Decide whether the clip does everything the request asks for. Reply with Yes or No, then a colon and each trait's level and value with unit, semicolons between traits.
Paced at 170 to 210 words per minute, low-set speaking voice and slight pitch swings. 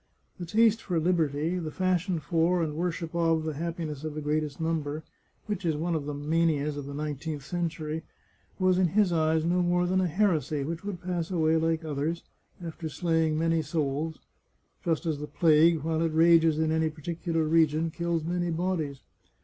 No: average, 185 wpm; medium, 160 Hz; narrow, 1.9 semitones